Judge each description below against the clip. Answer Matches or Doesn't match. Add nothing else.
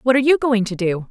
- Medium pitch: Doesn't match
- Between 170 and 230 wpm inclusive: Doesn't match